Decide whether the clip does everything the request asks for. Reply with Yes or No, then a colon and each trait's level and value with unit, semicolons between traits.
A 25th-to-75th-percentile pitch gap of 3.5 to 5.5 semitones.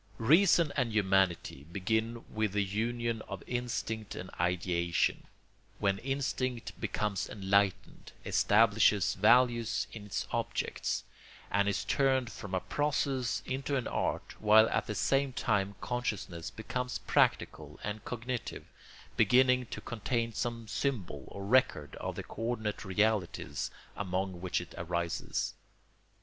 Yes: average, 4.0 semitones